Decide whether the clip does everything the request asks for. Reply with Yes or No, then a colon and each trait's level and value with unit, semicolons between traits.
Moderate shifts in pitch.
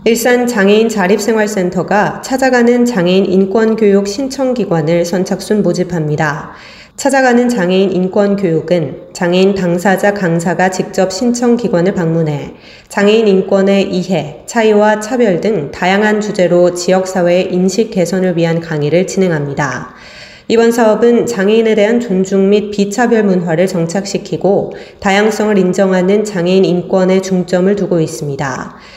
Yes: average, 3.2 semitones